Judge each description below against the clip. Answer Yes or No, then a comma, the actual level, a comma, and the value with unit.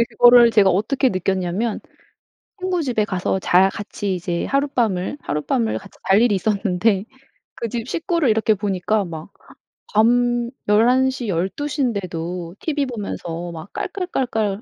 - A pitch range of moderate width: Yes, average, 4.8 semitones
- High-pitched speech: Yes, high, 210 Hz